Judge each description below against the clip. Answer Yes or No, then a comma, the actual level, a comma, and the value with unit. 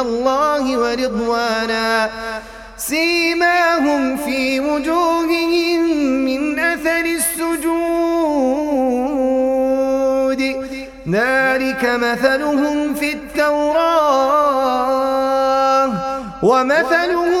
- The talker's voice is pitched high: Yes, very high, 270 Hz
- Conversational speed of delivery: No, slow, 45 wpm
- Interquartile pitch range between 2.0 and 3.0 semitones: No, average, 3.6 semitones